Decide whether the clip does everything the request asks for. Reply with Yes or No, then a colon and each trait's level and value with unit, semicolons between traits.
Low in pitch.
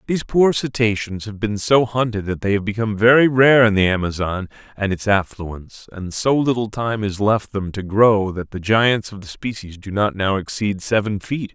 Yes: low, 105 Hz